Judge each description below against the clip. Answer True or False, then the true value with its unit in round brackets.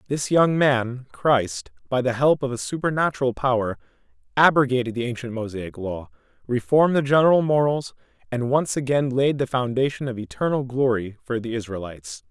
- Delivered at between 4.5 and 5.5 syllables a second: True (5.4 syllables/s)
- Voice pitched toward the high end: False (130 Hz)